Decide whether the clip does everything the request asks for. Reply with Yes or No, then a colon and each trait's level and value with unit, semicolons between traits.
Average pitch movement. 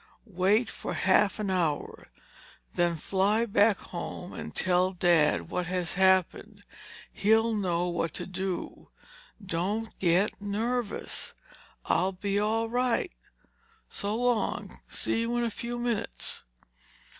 Yes: average, 3.7 semitones